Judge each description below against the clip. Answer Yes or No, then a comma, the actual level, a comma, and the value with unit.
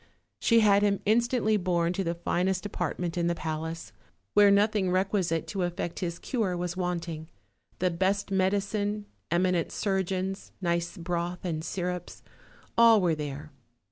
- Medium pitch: Yes, medium, 180 Hz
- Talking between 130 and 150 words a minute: Yes, average, 145 wpm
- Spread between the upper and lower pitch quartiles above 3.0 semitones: No, average, 2.7 semitones